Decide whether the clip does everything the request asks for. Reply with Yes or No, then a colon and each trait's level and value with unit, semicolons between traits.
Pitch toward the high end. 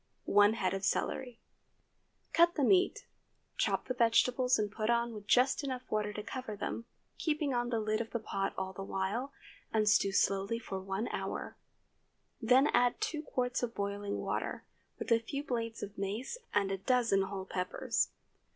Yes: high, 225 Hz